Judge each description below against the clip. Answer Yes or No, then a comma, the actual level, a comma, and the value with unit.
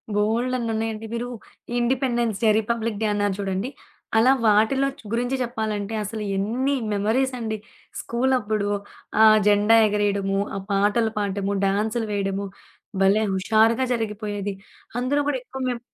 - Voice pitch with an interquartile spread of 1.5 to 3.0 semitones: Yes, average, 2.7 semitones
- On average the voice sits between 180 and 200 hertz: No, high, 220 Hz